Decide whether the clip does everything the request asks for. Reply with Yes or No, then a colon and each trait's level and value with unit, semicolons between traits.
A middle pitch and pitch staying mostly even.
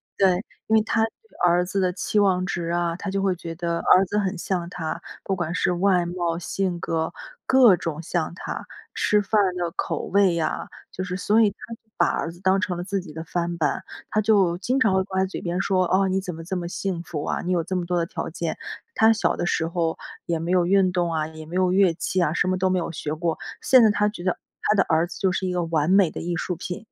Yes: medium, 180 Hz; narrow, 2.2 semitones